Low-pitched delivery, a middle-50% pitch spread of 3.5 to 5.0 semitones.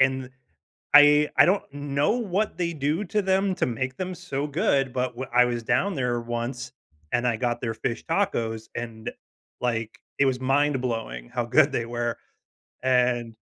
Yes: low, 130 Hz; average, 3.8 semitones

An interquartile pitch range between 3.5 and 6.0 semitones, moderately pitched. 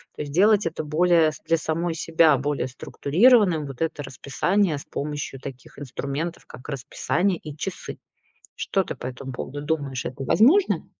Yes: average, 3.9 semitones; medium, 155 Hz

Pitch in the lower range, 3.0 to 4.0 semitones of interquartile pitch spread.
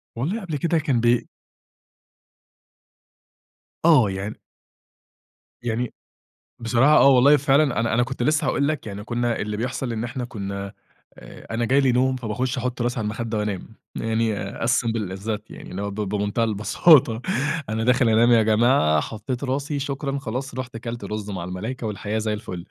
Yes: low, 115 Hz; average, 3.5 semitones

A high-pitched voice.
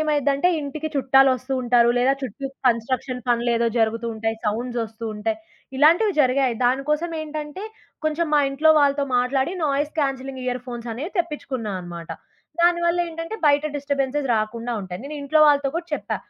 Yes: very high, 270 Hz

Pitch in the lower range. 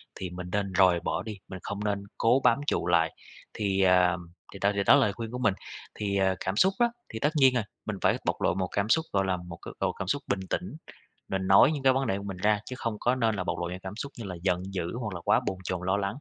Yes: low, 100 Hz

